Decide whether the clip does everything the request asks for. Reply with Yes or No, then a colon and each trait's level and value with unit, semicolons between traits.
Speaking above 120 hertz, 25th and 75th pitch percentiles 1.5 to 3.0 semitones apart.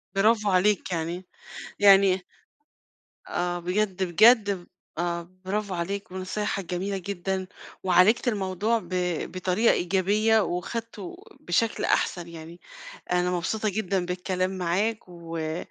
Yes: medium, 185 Hz; average, 2.7 semitones